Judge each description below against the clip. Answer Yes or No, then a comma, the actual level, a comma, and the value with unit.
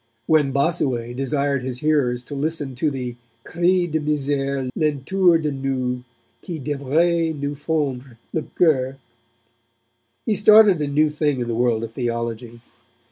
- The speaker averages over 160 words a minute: No, average, 140 wpm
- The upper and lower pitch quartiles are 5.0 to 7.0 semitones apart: No, average, 3.7 semitones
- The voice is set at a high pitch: No, medium, 140 Hz